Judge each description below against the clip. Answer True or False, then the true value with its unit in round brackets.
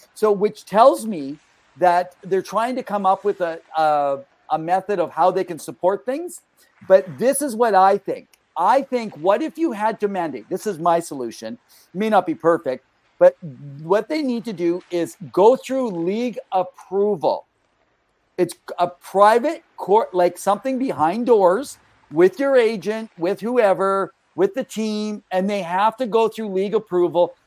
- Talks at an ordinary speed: True (170 wpm)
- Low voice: False (195 Hz)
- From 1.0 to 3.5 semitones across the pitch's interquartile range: False (4.3 semitones)